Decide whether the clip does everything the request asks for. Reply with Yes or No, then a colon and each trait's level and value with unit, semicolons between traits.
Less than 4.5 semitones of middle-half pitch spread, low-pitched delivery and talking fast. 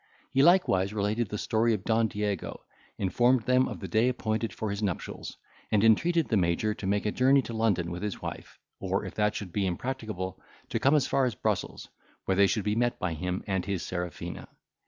Yes: average, 3.8 semitones; low, 105 Hz; fast, 210 wpm